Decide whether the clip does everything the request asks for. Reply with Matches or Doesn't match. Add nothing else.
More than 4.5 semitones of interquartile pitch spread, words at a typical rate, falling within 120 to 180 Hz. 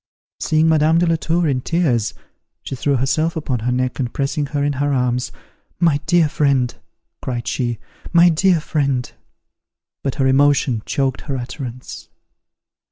Doesn't match